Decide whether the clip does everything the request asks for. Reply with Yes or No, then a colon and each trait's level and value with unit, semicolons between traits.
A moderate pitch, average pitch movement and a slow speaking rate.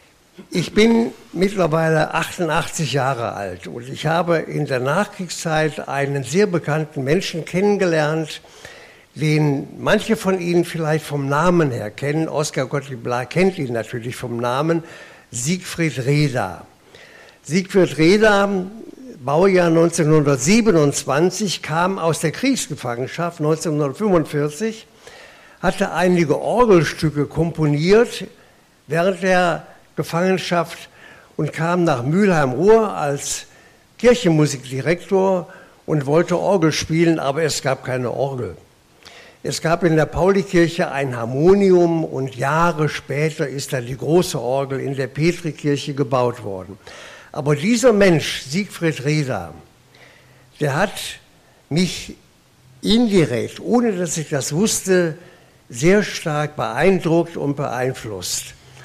Yes: medium, 160 Hz; average, 4.0 semitones; slow, 105 wpm